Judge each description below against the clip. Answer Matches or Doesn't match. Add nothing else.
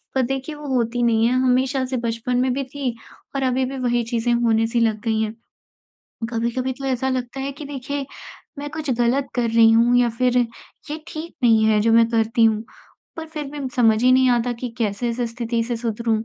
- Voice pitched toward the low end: Doesn't match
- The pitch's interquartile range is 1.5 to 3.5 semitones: Matches